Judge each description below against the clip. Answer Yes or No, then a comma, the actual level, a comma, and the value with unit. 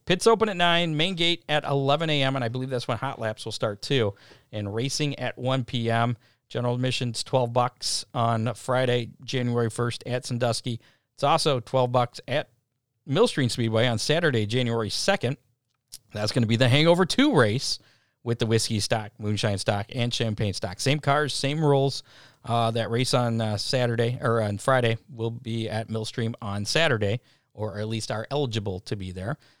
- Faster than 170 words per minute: Yes, average, 180 wpm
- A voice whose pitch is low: Yes, low, 120 Hz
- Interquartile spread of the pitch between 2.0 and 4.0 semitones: Yes, average, 3.0 semitones